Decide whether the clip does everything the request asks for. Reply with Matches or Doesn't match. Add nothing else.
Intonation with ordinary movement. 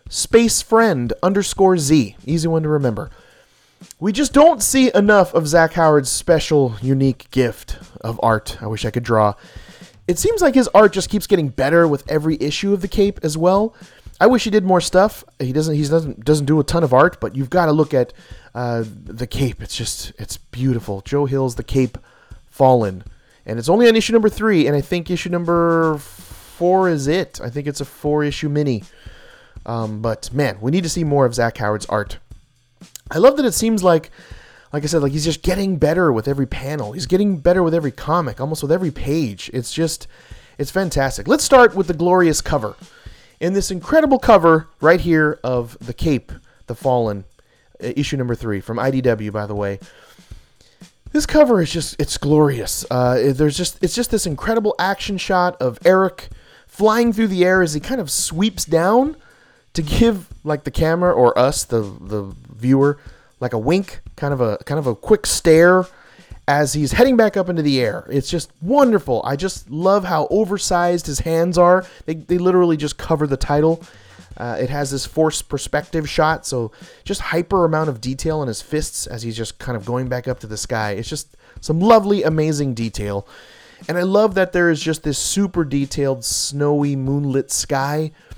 Doesn't match